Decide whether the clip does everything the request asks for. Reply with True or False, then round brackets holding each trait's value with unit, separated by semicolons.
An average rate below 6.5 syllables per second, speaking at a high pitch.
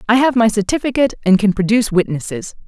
False (6.9 syllables/s; 215 Hz)